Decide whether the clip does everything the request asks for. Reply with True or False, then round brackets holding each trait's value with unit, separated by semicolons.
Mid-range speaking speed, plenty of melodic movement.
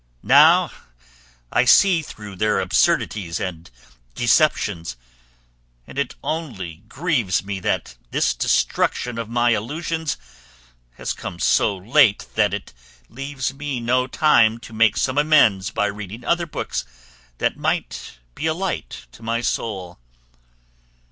False (130 wpm; 6.5 semitones)